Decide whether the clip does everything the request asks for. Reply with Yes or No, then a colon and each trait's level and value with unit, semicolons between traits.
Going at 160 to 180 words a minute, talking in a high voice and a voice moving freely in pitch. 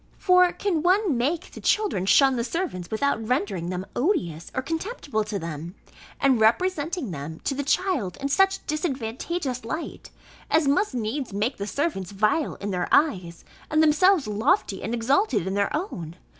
Yes: average, 165 wpm; very high, 260 Hz; wide, 8.4 semitones